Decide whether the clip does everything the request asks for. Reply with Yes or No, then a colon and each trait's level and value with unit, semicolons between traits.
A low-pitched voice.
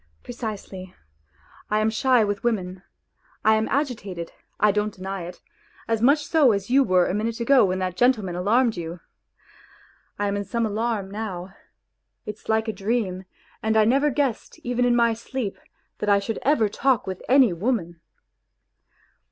No: high, 215 Hz